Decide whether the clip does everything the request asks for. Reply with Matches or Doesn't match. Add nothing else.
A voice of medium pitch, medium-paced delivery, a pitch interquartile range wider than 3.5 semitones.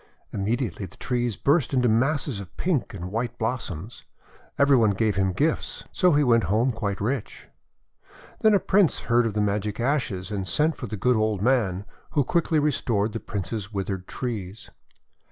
Doesn't match